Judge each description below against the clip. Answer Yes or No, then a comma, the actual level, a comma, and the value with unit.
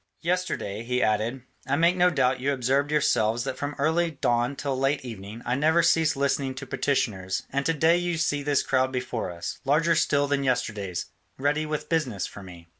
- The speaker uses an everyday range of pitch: Yes, average, 4.1 semitones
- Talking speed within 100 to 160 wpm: No, average, 190 wpm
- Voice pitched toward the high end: No, low, 135 Hz